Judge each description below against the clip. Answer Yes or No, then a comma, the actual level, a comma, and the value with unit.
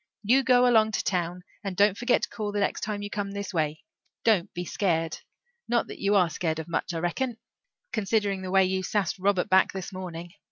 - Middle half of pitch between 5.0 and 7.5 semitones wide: No, average, 2.9 semitones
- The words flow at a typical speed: No, fast, 215 wpm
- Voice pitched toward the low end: No, high, 195 Hz